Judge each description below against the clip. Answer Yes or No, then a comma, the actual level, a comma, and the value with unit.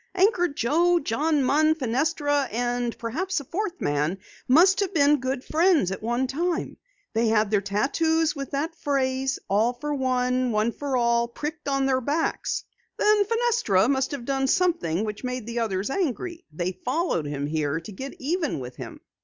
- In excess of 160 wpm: Yes, average, 170 wpm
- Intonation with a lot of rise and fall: Yes, wide, 5.8 semitones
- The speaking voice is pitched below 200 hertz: No, very high, 265 Hz